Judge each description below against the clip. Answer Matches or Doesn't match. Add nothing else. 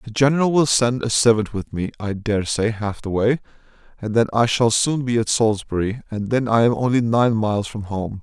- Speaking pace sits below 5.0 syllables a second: Doesn't match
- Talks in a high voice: Doesn't match